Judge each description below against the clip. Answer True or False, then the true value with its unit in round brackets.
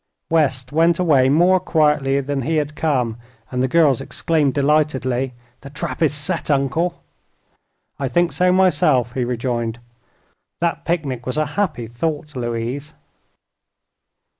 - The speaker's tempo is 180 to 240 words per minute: False (135 wpm)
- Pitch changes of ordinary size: True (4.0 semitones)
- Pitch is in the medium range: True (145 Hz)